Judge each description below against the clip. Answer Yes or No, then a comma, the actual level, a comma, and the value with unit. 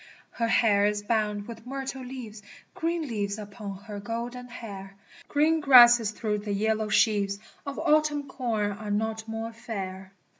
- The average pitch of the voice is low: No, high, 220 Hz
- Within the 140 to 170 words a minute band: Yes, average, 155 wpm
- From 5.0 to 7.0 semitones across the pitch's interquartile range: No, average, 3.2 semitones